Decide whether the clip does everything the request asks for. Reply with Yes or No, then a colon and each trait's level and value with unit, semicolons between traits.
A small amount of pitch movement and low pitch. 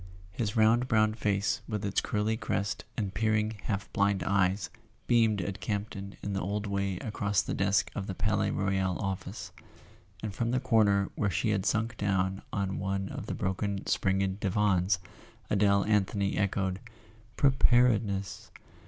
Yes: narrow, 1.8 semitones; low, 100 Hz